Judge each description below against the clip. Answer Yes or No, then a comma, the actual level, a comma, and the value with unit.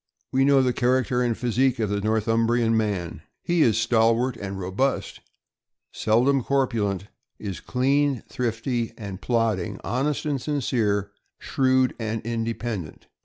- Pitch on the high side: No, low, 115 Hz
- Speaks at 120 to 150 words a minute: Yes, slow, 135 wpm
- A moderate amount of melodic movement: Yes, average, 3.2 semitones